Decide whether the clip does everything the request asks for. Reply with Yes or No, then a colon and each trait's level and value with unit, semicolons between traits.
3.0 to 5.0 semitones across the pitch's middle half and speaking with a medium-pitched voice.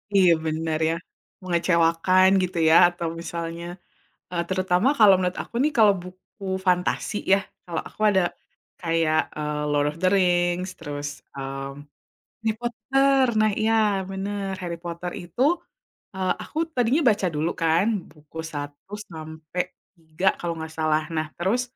Yes: average, 3.4 semitones; medium, 175 Hz